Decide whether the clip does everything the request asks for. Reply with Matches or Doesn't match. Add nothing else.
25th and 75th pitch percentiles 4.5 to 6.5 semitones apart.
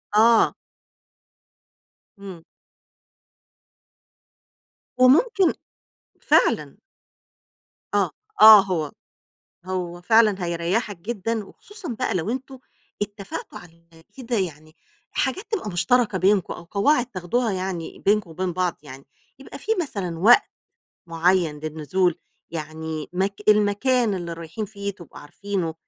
Matches